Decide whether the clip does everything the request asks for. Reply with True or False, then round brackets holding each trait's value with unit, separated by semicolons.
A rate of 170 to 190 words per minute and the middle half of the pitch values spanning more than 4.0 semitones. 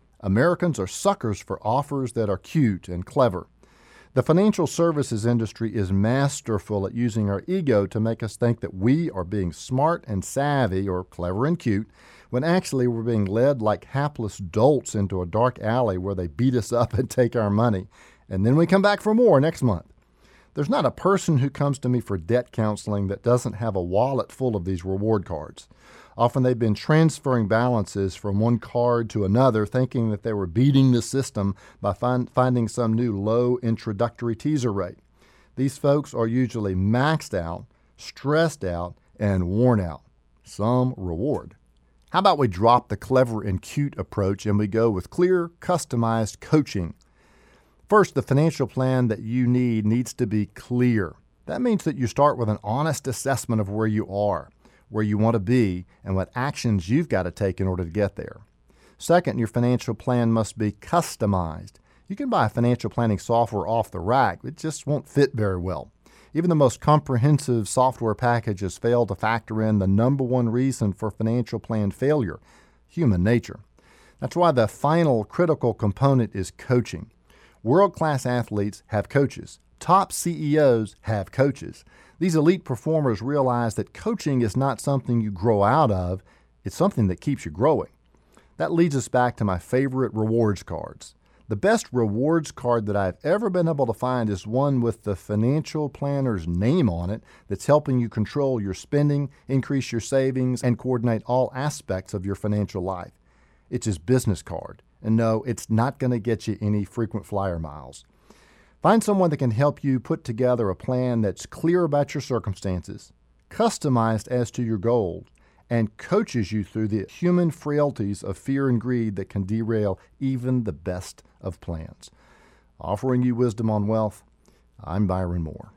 True (175 wpm; 4.5 semitones)